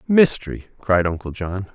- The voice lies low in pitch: Yes, low, 105 Hz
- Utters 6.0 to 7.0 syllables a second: No, 4.9 syllables/s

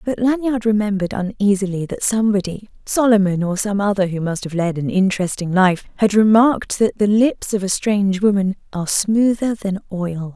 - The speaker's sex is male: No, female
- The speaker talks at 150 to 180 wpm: Yes, average, 160 wpm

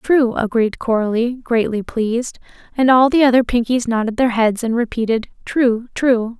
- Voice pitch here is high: Yes, high, 235 Hz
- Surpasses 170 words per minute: No, average, 150 wpm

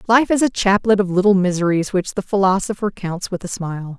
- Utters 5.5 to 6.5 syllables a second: Yes, 5.7 syllables/s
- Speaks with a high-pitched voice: Yes, high, 195 Hz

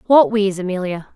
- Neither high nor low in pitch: No, high, 200 Hz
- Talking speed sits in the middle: Yes, average, 155 wpm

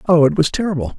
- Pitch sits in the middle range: Yes, medium, 160 Hz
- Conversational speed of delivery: No, fast, 245 wpm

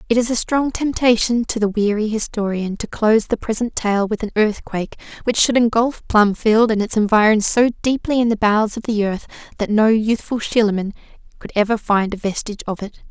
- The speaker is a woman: Yes, female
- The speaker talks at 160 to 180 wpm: No, average, 195 wpm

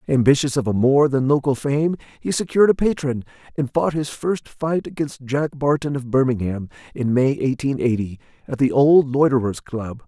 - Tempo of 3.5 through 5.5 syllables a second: Yes, 5.0 syllables/s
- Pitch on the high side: No, low, 135 Hz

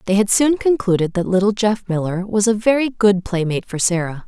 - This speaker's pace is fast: Yes, fast, 210 wpm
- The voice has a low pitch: No, high, 205 Hz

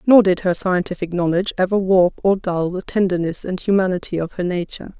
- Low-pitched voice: No, medium, 185 Hz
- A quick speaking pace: No, average, 190 wpm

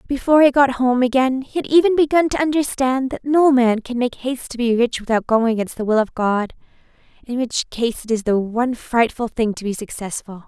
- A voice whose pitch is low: No, high, 245 Hz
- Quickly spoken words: Yes, fast, 225 wpm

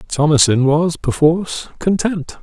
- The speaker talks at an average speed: No, slow, 100 wpm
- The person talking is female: No, male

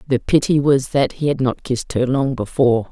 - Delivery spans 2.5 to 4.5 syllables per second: No, 5.6 syllables/s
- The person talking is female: Yes, female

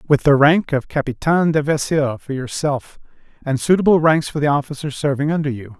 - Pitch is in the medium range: Yes, medium, 145 Hz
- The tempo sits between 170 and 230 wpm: Yes, average, 185 wpm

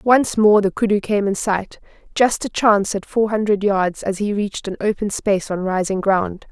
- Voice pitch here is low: No, high, 205 Hz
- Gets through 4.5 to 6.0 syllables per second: Yes, 5.0 syllables/s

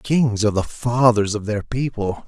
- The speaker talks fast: No, average, 185 wpm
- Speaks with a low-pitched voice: Yes, low, 115 Hz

